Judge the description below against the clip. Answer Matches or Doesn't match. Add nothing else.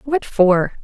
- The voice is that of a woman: Matches